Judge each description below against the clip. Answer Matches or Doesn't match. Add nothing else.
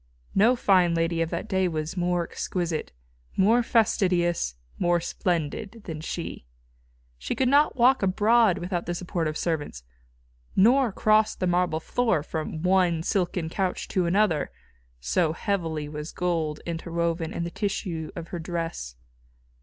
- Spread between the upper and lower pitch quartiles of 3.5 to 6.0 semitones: Doesn't match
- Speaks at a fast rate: Doesn't match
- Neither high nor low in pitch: Matches